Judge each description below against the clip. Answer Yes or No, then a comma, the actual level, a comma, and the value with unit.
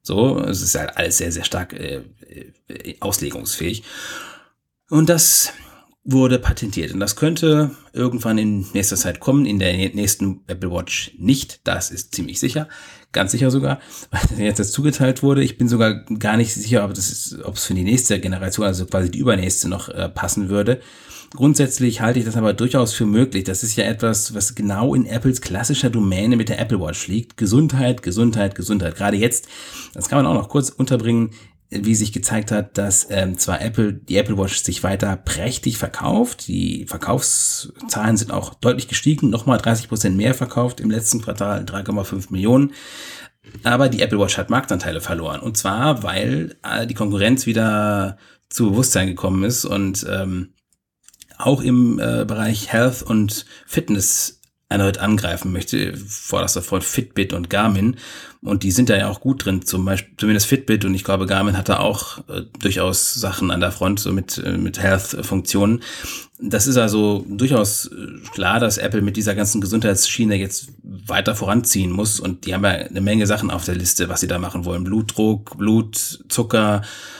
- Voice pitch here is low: Yes, low, 105 Hz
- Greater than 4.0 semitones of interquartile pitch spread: No, average, 3.7 semitones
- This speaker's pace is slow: No, average, 175 wpm